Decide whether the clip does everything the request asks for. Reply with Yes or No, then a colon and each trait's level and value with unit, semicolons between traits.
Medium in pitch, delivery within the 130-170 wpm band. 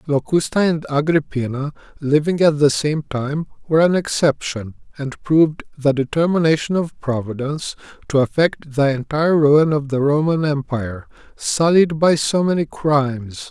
Yes: medium, 150 Hz; average, 140 wpm